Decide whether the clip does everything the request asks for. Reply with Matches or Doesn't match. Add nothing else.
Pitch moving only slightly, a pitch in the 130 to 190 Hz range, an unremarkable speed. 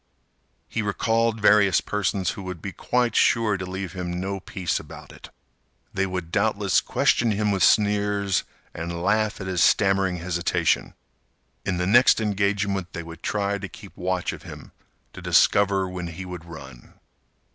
Doesn't match